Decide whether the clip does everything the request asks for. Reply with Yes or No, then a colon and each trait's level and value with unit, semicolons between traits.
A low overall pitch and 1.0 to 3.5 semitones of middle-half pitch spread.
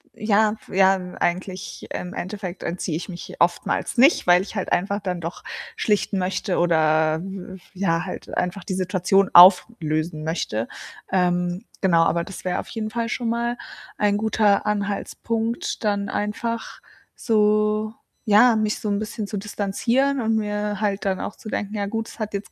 No: high, 200 Hz; average, 3.1 semitones